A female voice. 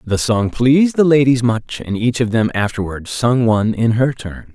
No: male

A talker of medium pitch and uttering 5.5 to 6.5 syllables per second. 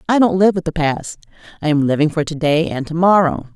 Yes: medium, 165 Hz; 5.9 syllables/s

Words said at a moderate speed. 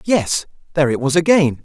Yes: average, 185 wpm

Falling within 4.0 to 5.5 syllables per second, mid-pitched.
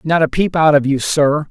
Yes: 5.0 syllables/s; medium, 150 Hz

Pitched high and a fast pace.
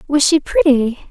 No: very high, 295 Hz; average, 165 wpm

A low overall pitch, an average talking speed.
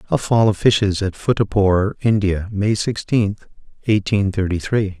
Yes: low, 100 Hz; average, 145 wpm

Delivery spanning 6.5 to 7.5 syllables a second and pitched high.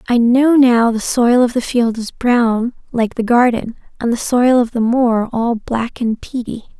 No: 4.1 syllables/s; high, 235 Hz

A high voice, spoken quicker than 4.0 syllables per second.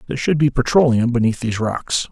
No: low, 125 Hz; 6.3 syllables/s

